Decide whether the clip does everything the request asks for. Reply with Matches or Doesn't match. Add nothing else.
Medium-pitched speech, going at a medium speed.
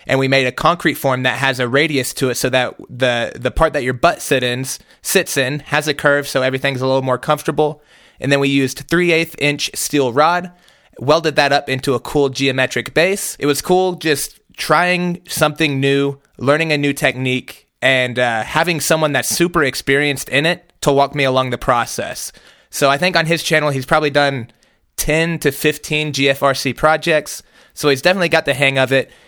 Matches